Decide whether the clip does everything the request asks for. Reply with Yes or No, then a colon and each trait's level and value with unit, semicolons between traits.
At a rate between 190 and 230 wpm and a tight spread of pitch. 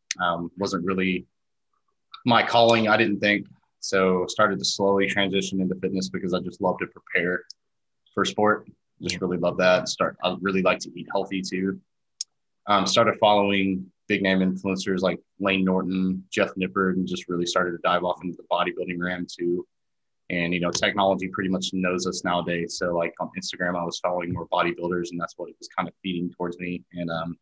Yes: average, 195 wpm; narrow, 1.5 semitones